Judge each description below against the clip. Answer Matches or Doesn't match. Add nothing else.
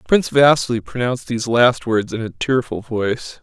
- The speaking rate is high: Doesn't match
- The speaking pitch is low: Matches